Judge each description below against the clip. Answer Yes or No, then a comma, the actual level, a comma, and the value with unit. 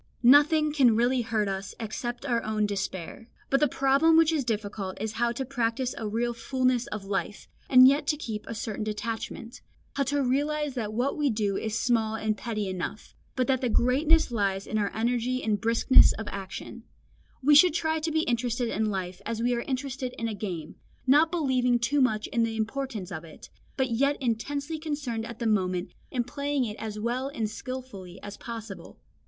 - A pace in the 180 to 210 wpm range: Yes, average, 195 wpm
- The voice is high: Yes, high, 235 Hz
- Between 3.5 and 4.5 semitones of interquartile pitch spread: Yes, average, 3.9 semitones